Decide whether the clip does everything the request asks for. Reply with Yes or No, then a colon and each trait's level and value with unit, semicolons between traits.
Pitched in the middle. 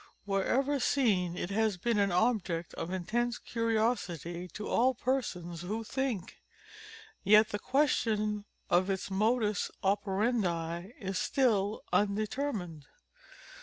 No: high, 205 Hz